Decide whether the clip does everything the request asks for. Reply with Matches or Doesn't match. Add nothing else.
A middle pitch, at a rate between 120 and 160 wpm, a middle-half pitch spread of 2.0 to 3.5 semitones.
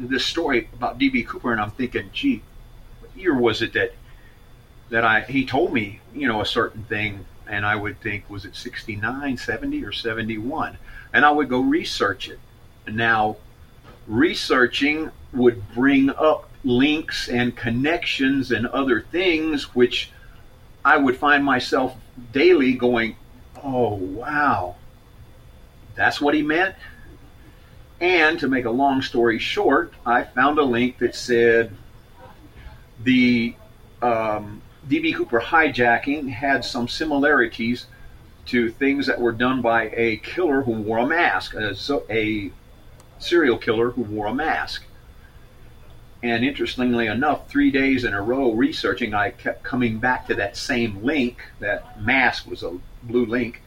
Doesn't match